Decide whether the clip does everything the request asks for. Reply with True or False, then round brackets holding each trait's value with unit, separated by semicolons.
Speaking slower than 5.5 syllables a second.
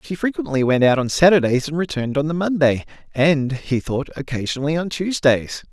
False (5.6 syllables/s)